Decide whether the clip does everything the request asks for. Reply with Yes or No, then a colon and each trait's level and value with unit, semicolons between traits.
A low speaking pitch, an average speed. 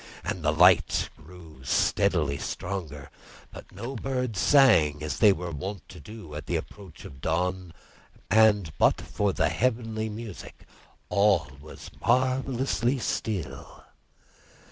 No: very low, 95 Hz; slow, 125 wpm